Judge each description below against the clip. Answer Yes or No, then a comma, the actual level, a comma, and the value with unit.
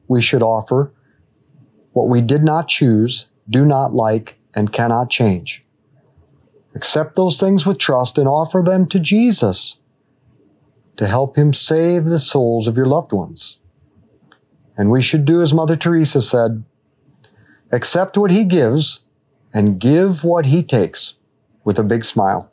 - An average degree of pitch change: No, wide, 5.9 semitones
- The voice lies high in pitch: No, low, 135 Hz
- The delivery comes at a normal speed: Yes, average, 145 wpm